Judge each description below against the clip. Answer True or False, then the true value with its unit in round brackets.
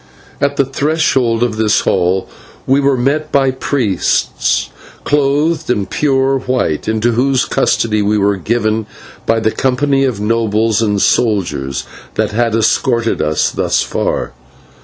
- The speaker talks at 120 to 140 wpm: True (135 wpm)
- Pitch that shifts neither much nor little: True (4.3 semitones)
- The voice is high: False (115 Hz)